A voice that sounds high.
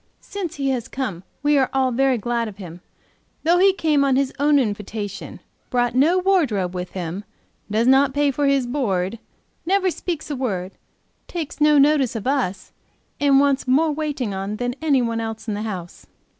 Yes: very high, 260 Hz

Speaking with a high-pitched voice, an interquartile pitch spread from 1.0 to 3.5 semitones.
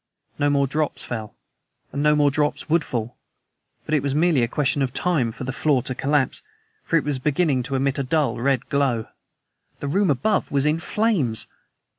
No: medium, 140 Hz; average, 2.7 semitones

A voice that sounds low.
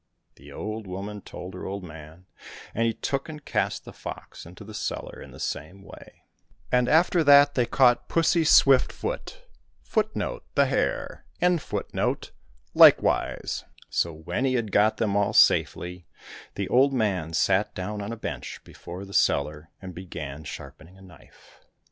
Yes: low, 100 Hz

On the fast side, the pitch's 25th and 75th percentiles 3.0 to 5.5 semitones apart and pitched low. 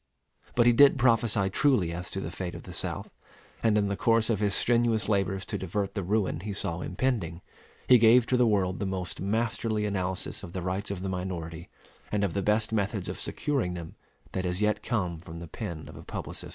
Yes: fast, 220 wpm; average, 3.6 semitones; low, 100 Hz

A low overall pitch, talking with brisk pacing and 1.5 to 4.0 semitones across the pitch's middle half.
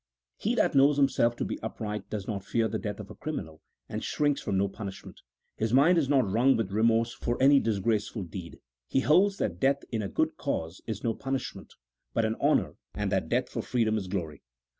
No: low, 110 Hz; fast, 210 wpm; average, 5.1 semitones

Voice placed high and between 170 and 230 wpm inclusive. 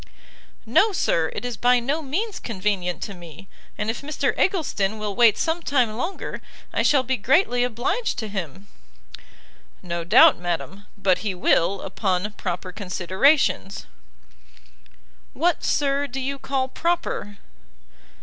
No: high, 225 Hz; slow, 135 wpm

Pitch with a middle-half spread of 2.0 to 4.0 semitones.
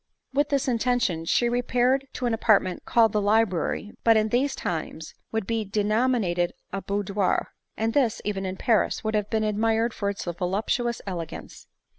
Yes: average, 3.3 semitones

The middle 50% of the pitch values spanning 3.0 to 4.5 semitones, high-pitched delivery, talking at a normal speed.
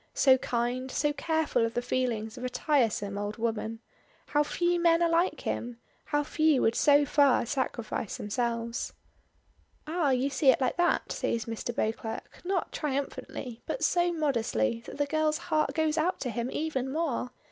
No: average, 4.9 semitones; very high, 265 Hz; average, 170 wpm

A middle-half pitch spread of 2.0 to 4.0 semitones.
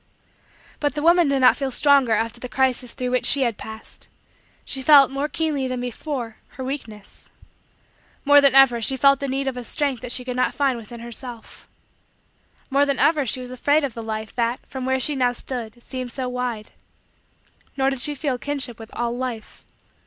Yes: narrow, 2.5 semitones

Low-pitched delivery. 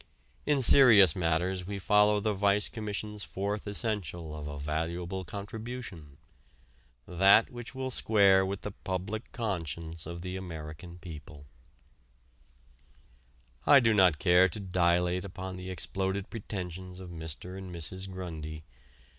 Yes: very low, 95 Hz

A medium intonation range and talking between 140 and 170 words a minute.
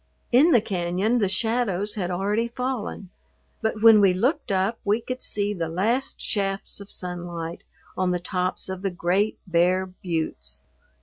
Yes: average, 3.7 semitones; average, 160 wpm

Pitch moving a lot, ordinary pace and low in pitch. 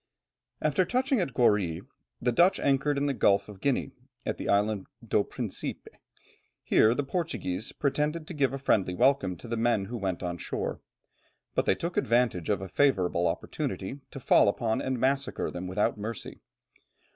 Yes: wide, 6.1 semitones; average, 170 wpm; low, 120 Hz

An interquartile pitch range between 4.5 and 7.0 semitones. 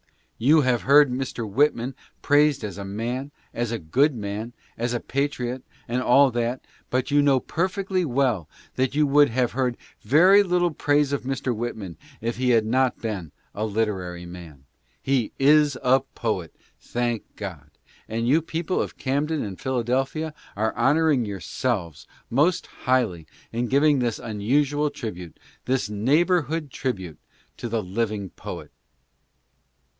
Yes: average, 4.8 semitones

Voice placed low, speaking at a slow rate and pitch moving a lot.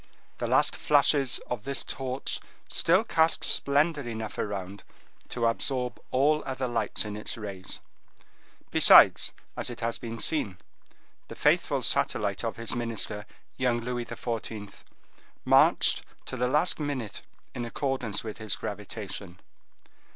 No: low, 120 Hz; slow, 130 wpm; average, 3.9 semitones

